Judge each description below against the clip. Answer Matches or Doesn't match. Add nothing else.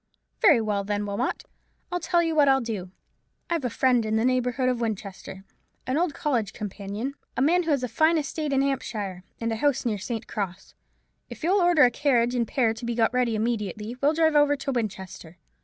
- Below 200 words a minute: Doesn't match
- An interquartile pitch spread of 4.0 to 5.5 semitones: Matches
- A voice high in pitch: Matches